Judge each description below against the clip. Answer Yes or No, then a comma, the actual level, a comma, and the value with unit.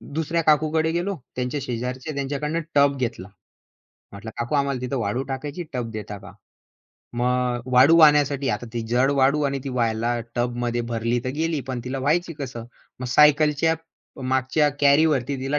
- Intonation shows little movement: No, average, 3.5 semitones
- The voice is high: No, low, 135 Hz